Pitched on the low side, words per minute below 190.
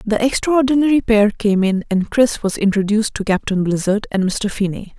No: high, 215 Hz; average, 180 wpm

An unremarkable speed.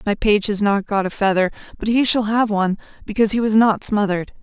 No: fast, 230 wpm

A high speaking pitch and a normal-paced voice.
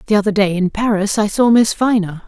No: high, 205 Hz; fast, 235 wpm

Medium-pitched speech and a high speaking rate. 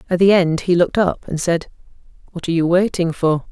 Yes: medium, 175 Hz; fast, 220 wpm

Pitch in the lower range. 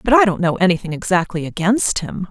No: high, 190 Hz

